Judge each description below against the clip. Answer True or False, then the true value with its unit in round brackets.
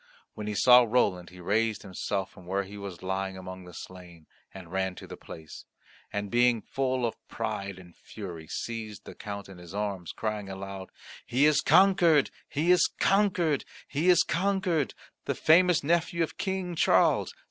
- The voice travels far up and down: True (8.3 semitones)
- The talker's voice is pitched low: True (105 Hz)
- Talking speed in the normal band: True (170 wpm)